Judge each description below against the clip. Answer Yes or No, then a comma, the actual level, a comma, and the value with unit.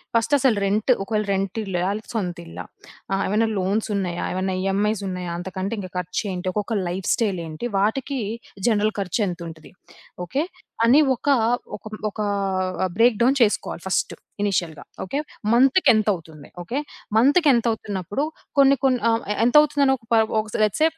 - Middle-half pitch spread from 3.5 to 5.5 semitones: Yes, average, 4.1 semitones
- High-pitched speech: Yes, high, 210 Hz